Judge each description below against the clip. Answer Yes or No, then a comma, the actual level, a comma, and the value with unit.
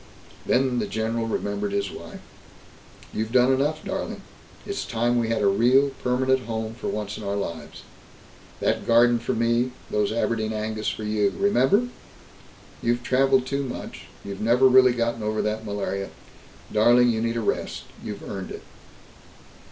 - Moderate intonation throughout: Yes, average, 3.0 semitones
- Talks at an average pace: Yes, average, 160 wpm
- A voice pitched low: Yes, low, 115 Hz